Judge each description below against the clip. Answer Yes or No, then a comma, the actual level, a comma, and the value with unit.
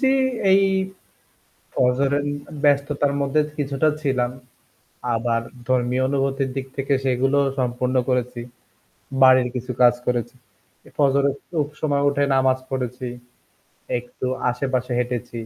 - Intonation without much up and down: Yes, narrow, 2.1 semitones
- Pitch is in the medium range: No, low, 130 Hz